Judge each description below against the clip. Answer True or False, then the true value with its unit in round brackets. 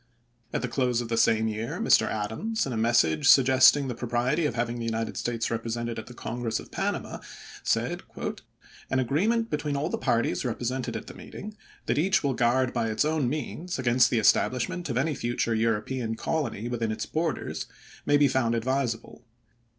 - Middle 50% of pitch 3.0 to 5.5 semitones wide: True (3.5 semitones)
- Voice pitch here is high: False (120 Hz)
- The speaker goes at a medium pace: True (180 wpm)